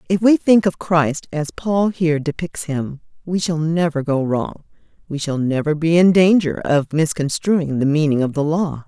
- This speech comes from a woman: Yes, female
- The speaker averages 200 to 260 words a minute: No, average, 190 wpm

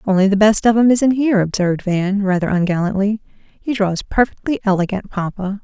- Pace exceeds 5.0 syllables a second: Yes, 5.5 syllables/s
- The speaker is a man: No, female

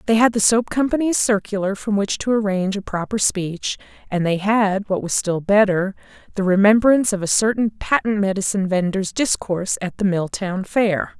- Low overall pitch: No, high, 200 Hz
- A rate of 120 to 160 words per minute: No, average, 175 wpm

